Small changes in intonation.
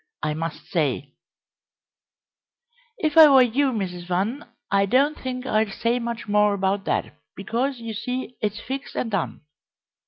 No: average, 4.8 semitones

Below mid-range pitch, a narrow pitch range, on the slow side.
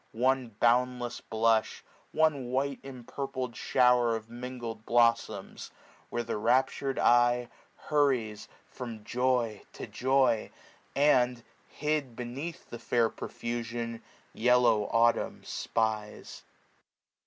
Yes: low, 120 Hz; narrow, 2.0 semitones; slow, 105 wpm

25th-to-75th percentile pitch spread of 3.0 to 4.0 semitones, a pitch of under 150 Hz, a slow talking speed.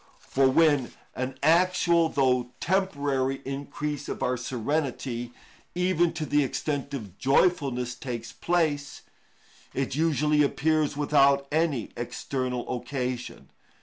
Yes: average, 3.4 semitones; medium, 140 Hz; slow, 115 wpm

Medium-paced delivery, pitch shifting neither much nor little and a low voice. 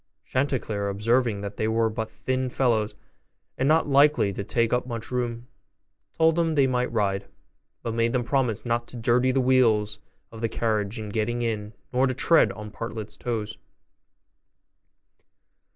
Yes: average, 160 wpm; average, 3.0 semitones; low, 115 Hz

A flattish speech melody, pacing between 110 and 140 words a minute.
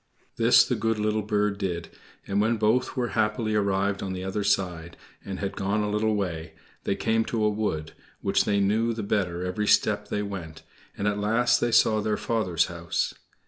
No: narrow, 2.1 semitones; average, 195 wpm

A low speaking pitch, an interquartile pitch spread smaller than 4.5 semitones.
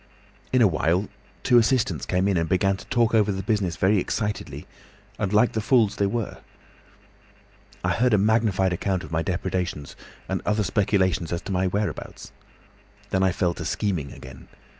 Yes: very low, 95 Hz; average, 2.8 semitones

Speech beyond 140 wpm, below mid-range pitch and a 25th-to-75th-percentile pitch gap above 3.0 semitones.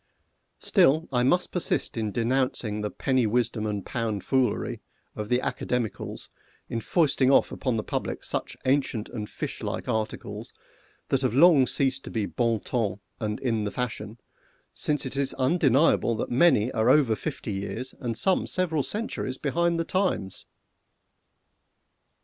Yes: average, 150 wpm; low, 125 Hz; average, 4.0 semitones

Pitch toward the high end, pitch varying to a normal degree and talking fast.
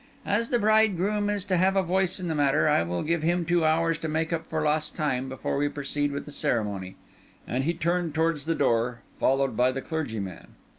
No: medium, 155 Hz; average, 4.5 semitones; fast, 215 wpm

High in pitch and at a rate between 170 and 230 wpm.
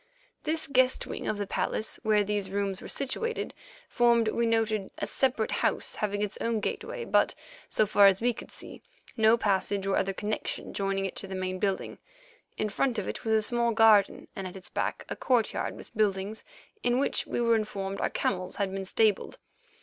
Yes: high, 210 Hz; average, 195 wpm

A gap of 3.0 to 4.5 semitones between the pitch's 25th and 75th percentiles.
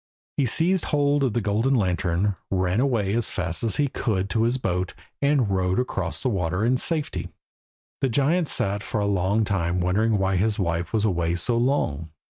No: wide, 5.5 semitones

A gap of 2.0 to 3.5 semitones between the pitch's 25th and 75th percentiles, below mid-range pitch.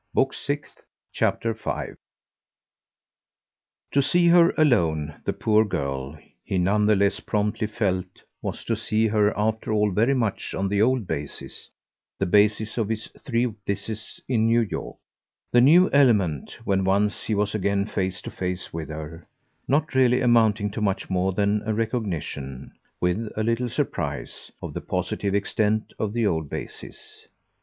Yes: average, 3.1 semitones; low, 105 Hz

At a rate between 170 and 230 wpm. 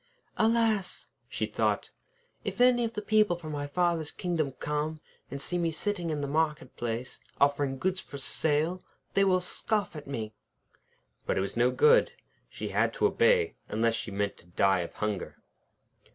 Yes: average, 175 wpm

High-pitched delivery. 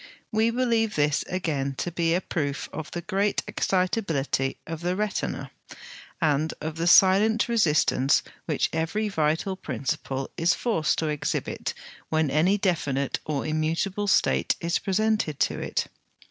No: medium, 165 Hz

